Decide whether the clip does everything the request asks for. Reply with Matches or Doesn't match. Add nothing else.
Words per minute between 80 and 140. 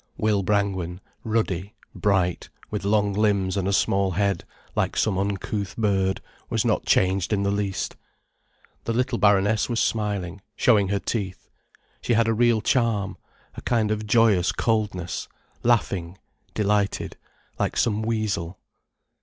Matches